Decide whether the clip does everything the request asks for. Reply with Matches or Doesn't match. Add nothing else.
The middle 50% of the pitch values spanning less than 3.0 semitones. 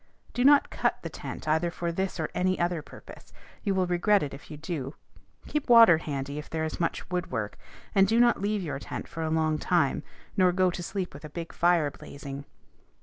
Doesn't match